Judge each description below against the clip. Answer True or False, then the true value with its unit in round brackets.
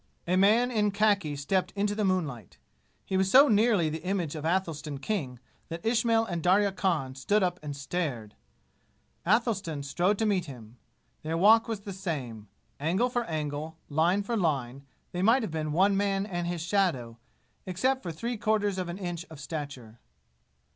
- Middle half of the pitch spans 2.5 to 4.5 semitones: False (5.2 semitones)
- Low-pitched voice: False (180 Hz)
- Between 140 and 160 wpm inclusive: False (175 wpm)